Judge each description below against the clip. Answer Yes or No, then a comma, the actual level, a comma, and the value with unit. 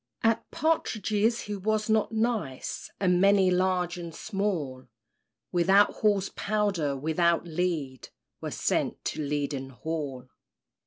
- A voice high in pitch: No, medium, 180 Hz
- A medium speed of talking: No, slow, 115 wpm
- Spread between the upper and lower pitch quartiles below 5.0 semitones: No, average, 5.3 semitones